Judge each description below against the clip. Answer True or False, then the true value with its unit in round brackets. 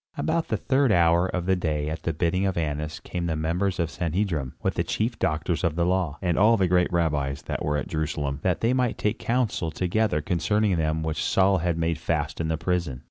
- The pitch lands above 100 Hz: False (85 Hz)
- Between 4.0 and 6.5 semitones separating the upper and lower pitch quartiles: False (3.3 semitones)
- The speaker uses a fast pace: True (230 wpm)